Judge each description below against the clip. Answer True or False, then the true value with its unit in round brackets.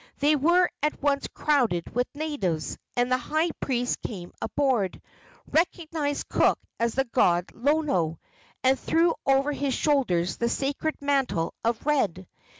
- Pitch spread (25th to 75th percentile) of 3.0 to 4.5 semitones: False (5.0 semitones)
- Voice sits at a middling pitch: False (270 Hz)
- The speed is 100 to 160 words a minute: True (140 wpm)